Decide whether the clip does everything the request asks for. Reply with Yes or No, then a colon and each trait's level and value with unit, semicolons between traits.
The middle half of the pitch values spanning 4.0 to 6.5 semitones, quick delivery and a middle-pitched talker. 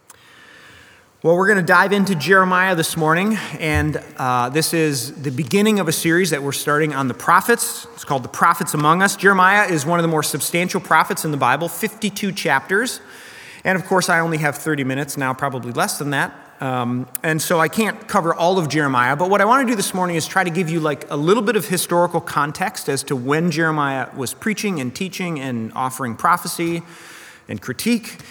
Yes: average, 4.3 semitones; fast, 210 wpm; medium, 165 Hz